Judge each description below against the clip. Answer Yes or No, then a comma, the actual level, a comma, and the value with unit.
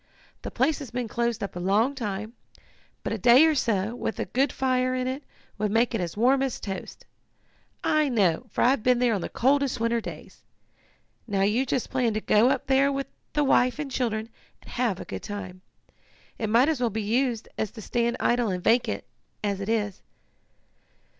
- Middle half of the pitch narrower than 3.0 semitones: No, average, 3.6 semitones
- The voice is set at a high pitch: Yes, high, 235 Hz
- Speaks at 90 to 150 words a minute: No, average, 200 wpm